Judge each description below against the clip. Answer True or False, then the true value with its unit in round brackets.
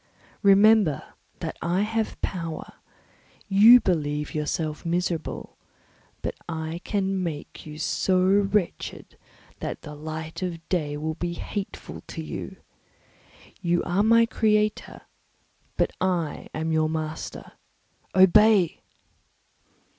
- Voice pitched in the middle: True (175 Hz)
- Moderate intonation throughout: True (4.0 semitones)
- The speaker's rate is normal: False (110 wpm)